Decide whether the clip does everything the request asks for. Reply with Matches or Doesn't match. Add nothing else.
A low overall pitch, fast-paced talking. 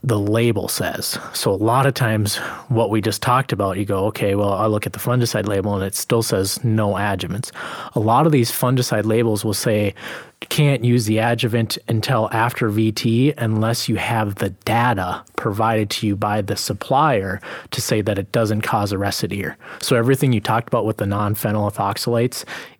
Doesn't match